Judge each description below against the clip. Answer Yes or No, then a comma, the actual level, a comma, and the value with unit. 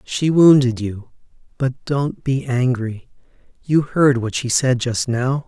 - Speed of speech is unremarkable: Yes, average, 155 wpm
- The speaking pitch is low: Yes, low, 130 Hz